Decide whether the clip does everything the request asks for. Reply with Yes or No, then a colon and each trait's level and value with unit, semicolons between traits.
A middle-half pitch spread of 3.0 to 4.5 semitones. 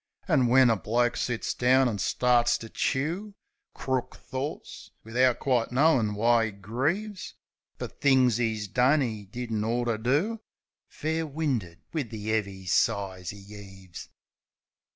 Yes: average, 3.8 semitones